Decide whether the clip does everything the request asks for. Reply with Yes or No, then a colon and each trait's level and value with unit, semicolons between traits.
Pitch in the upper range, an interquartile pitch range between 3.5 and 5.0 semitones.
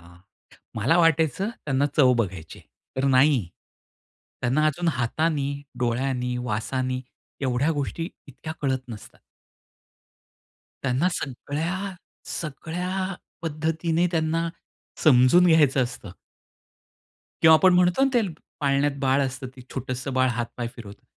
No: medium, 140 Hz; average, 4.3 semitones